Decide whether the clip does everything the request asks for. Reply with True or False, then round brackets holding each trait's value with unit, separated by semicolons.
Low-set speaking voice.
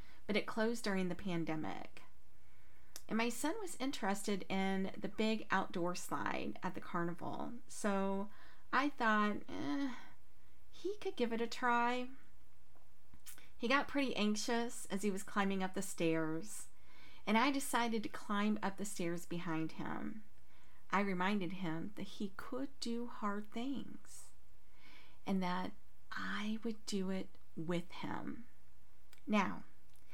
False (210 Hz)